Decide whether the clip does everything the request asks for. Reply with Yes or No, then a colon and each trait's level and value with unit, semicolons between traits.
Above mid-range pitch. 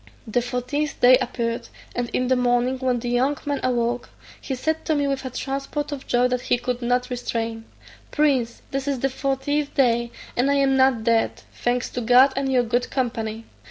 Yes: very high, 250 Hz